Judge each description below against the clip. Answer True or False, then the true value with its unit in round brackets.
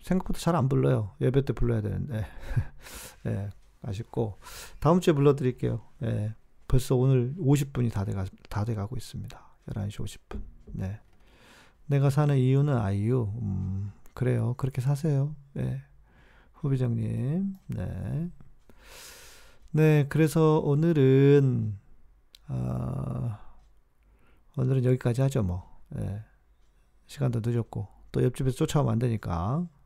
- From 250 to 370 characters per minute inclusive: False (235 characters per minute)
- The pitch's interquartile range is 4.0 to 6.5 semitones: True (5.5 semitones)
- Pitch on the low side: True (125 Hz)